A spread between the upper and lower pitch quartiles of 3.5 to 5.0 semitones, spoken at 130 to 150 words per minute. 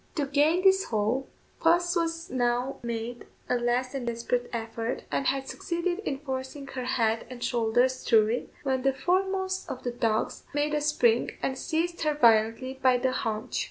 No: average, 4.1 semitones; average, 170 wpm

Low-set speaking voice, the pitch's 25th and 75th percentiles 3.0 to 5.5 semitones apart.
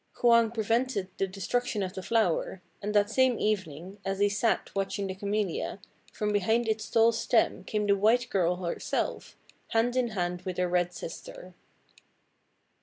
No: high, 205 Hz; average, 3.3 semitones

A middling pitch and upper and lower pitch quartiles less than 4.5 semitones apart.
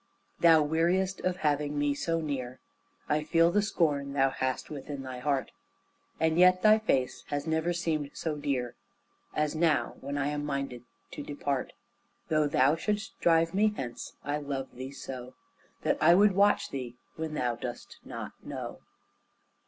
Yes: medium, 150 Hz; average, 3.5 semitones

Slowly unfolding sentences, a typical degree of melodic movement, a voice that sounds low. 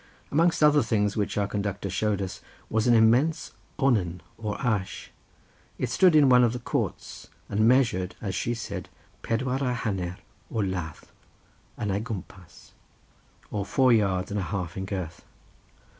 No: average, 160 wpm; average, 4.4 semitones; low, 105 Hz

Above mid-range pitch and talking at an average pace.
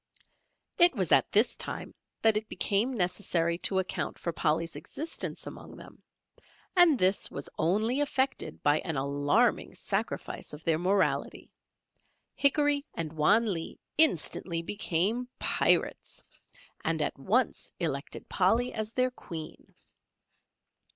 No: high, 195 Hz; slow, 125 wpm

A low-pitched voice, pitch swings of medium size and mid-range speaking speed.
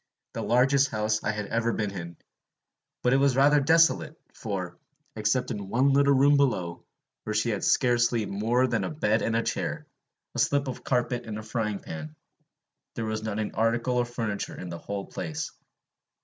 Yes: low, 115 Hz; average, 3.6 semitones; average, 185 wpm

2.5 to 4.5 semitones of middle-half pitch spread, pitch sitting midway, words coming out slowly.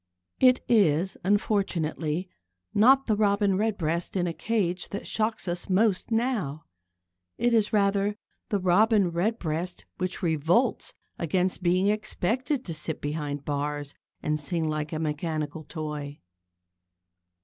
No: average, 5.2 semitones; medium, 180 Hz; slow, 125 wpm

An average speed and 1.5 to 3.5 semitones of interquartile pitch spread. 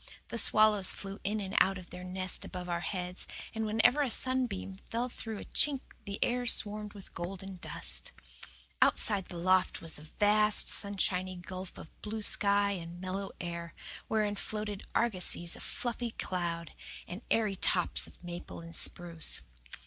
Yes: average, 165 wpm; average, 3.2 semitones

